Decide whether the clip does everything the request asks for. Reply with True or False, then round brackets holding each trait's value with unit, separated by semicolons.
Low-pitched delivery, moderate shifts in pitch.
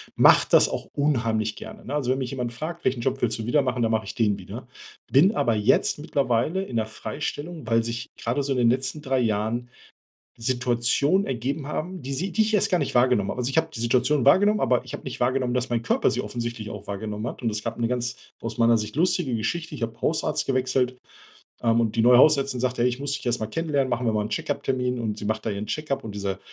True (125 Hz; 3.5 semitones)